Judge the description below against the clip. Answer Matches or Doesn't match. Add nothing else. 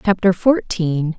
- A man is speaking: Doesn't match